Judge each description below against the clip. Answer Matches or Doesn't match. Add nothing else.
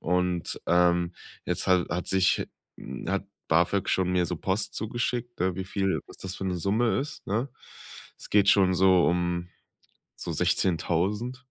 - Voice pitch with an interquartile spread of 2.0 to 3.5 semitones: Matches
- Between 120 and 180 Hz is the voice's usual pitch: Doesn't match